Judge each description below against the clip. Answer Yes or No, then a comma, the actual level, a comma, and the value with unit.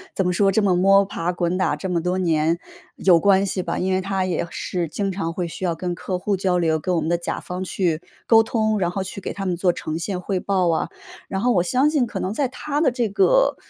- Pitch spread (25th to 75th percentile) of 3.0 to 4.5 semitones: No, narrow, 2.4 semitones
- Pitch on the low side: No, medium, 185 Hz